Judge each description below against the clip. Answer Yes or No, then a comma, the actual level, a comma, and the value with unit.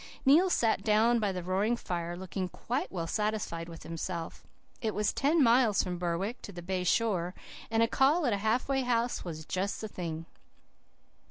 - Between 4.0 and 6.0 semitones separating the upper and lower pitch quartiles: Yes, average, 4.9 semitones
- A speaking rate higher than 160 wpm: Yes, average, 185 wpm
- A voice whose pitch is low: No, high, 205 Hz